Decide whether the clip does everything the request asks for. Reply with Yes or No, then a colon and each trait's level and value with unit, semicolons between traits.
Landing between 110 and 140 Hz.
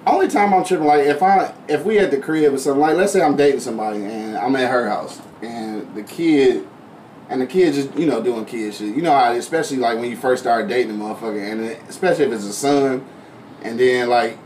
Yes: low, 135 Hz